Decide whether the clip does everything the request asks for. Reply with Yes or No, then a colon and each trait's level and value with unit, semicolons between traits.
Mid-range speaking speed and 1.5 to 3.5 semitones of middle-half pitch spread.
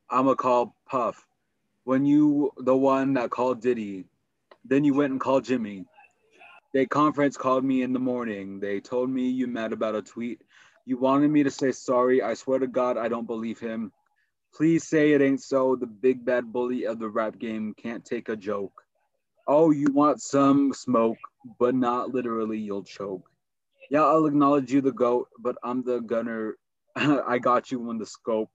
Yes: average, 185 wpm; average, 2.9 semitones